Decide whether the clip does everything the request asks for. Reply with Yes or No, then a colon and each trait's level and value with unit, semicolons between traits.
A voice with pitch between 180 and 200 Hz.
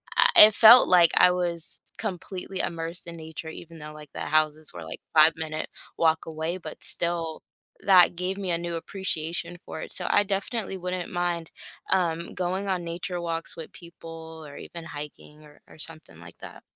No: medium, 170 Hz